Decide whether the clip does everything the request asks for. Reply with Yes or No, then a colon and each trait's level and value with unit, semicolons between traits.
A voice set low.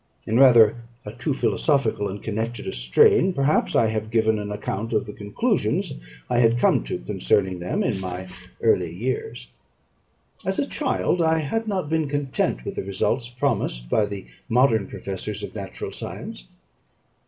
Yes: low, 110 Hz